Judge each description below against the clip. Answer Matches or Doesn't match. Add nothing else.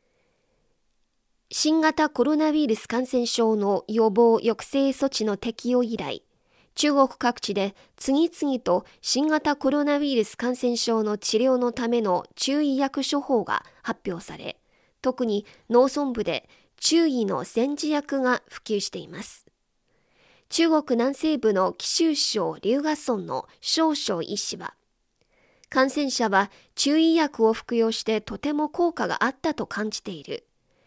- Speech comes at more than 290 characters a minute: Doesn't match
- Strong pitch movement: Doesn't match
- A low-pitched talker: Doesn't match